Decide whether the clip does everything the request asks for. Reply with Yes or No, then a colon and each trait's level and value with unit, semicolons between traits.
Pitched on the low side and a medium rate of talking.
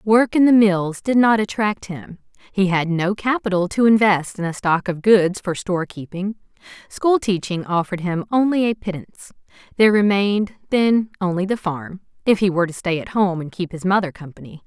No: high, 195 Hz; average, 190 wpm